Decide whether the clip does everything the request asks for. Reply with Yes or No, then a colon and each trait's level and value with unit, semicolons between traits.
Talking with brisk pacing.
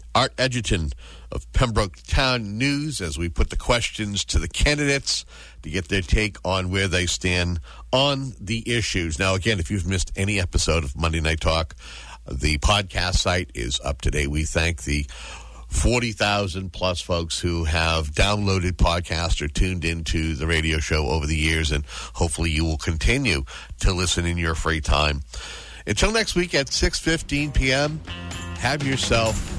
No: average, 165 wpm